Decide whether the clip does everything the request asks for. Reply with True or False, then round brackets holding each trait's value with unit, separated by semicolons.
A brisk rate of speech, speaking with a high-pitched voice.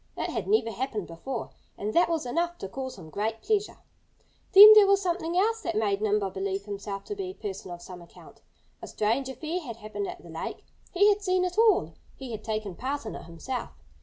True (220 wpm; 255 Hz)